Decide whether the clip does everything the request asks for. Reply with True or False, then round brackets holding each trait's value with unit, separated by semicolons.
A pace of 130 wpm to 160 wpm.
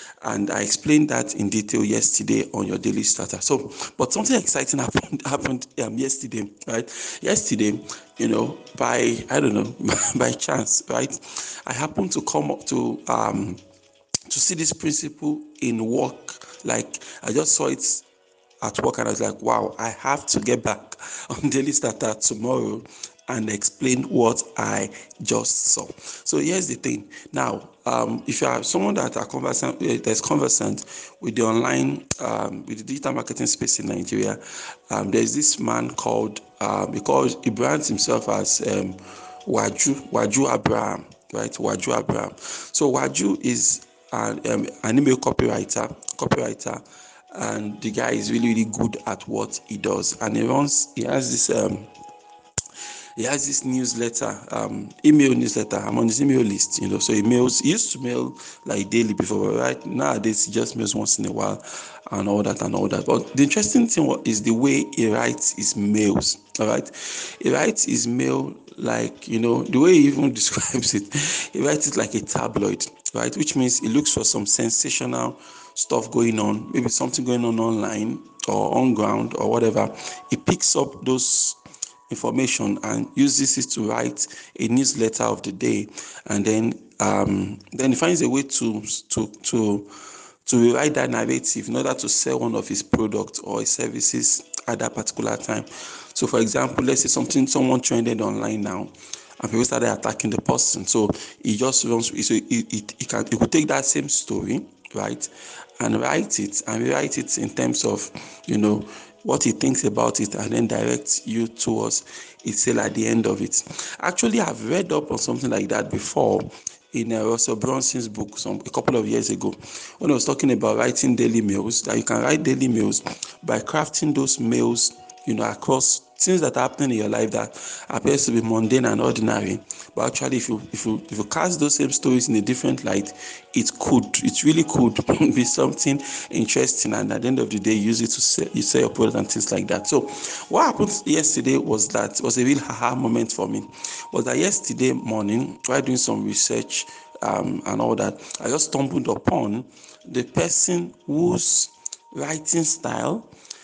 False (185 wpm)